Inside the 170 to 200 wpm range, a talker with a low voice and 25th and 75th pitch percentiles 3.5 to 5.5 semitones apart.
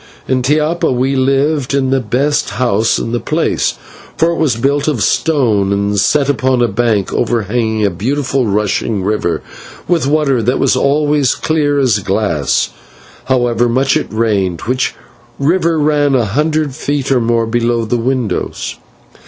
No: average, 155 wpm; low, 125 Hz; average, 4.4 semitones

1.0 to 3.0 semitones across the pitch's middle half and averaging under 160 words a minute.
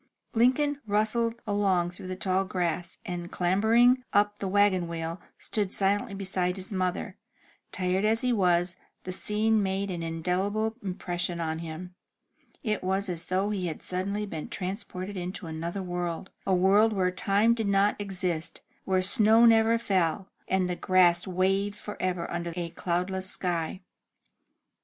Yes: narrow, 2.5 semitones; average, 150 wpm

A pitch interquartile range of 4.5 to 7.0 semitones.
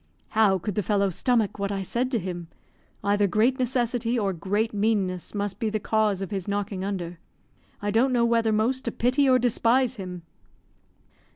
No: average, 3.3 semitones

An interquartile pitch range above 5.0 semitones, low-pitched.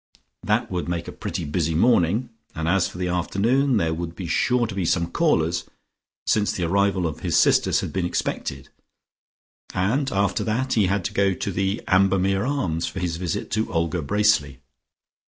No: average, 3.6 semitones; very low, 95 Hz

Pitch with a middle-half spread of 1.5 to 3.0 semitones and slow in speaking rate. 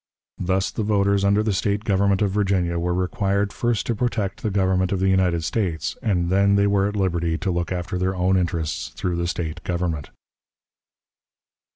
No: narrow, 2.4 semitones; average, 185 wpm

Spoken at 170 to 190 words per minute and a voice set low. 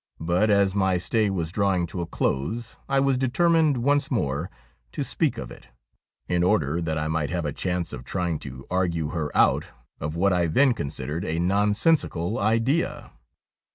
Yes: average, 180 wpm; very low, 90 Hz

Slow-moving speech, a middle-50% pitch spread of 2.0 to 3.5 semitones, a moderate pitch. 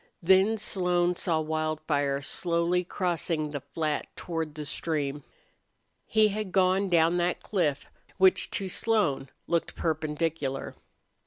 Yes: slow, 115 wpm; average, 3.2 semitones; medium, 170 Hz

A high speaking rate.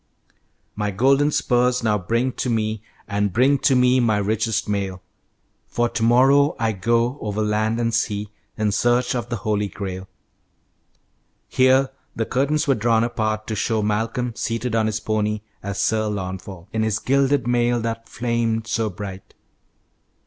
No: average, 155 wpm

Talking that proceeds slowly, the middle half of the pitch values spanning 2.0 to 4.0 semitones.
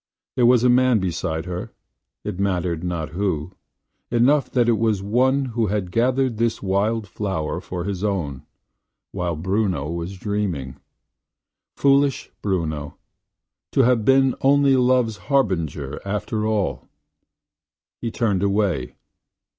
No: slow, 130 wpm; average, 5.3 semitones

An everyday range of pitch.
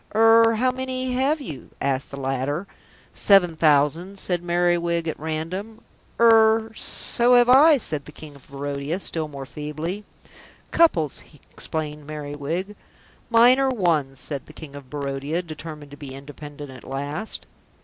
No: wide, 7.4 semitones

